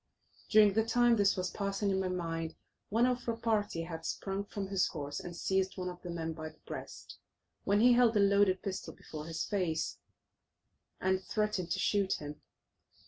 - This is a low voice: No, high, 190 Hz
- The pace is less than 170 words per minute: No, average, 190 wpm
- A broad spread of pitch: No, average, 3.4 semitones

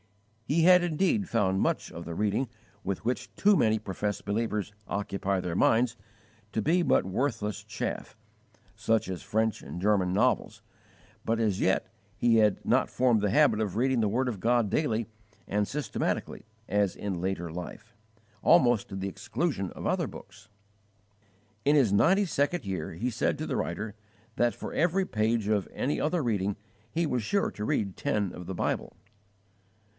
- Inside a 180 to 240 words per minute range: No, average, 170 wpm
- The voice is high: No, low, 110 Hz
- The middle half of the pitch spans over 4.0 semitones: Yes, average, 4.6 semitones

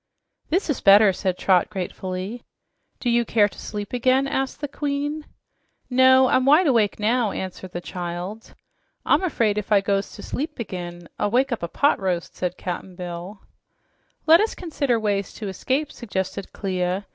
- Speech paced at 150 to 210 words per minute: Yes, average, 170 wpm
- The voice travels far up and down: Yes, wide, 5.8 semitones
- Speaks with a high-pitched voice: Yes, high, 210 Hz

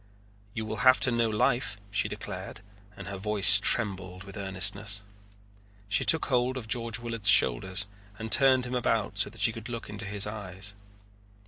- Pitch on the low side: Yes, low, 105 Hz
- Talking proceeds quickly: No, average, 175 wpm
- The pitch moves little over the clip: No, average, 3.0 semitones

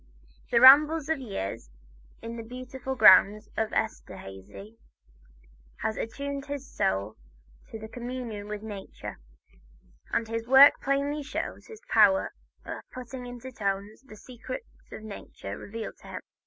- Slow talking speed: Yes, slow, 130 wpm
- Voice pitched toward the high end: Yes, high, 230 Hz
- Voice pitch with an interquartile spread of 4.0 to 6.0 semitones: Yes, average, 4.3 semitones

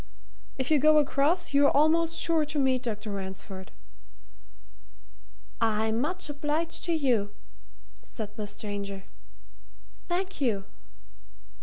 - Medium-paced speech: No, slow, 110 wpm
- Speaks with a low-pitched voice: No, very high, 275 Hz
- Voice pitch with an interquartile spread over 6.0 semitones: Yes, wide, 6.7 semitones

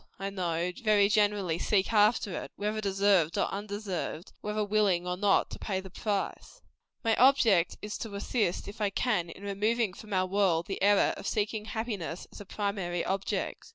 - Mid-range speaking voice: No, high, 200 Hz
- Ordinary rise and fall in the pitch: No, narrow, 2.3 semitones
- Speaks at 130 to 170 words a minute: No, average, 185 wpm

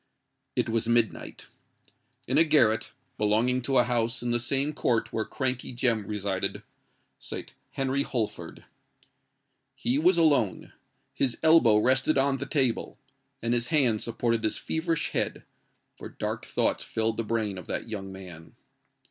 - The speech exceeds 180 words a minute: No, average, 145 wpm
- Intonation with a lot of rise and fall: No, average, 3.5 semitones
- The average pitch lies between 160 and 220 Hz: No, low, 120 Hz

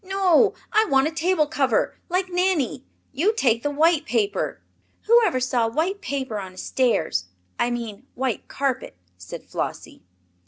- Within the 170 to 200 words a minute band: No, average, 150 wpm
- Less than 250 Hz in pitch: No, very high, 275 Hz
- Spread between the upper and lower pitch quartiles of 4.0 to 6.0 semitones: No, wide, 6.9 semitones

